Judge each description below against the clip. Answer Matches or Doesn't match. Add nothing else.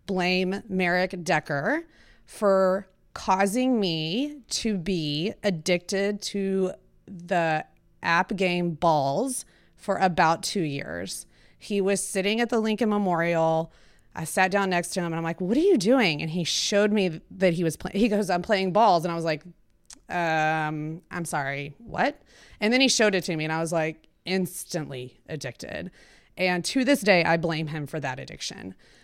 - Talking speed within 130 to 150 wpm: Doesn't match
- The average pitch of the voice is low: Doesn't match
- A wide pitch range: Doesn't match